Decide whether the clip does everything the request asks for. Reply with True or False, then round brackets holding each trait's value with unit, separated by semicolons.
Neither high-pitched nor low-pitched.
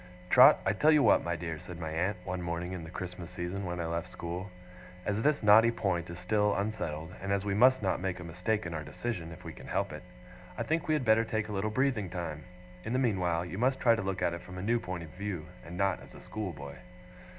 False (95 Hz)